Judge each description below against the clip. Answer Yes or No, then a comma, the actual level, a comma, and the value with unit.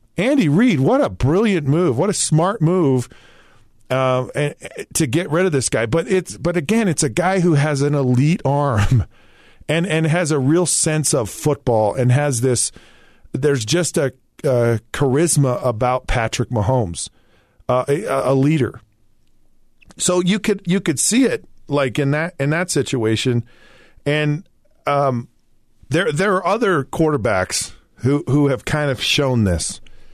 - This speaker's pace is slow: No, average, 160 wpm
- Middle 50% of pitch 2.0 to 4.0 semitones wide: No, average, 4.8 semitones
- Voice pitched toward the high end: No, medium, 140 Hz